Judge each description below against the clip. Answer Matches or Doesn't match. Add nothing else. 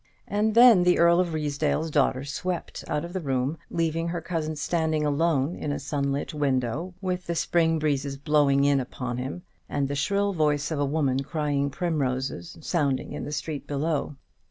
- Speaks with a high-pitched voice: Doesn't match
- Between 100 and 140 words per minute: Doesn't match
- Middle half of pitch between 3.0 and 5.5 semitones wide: Matches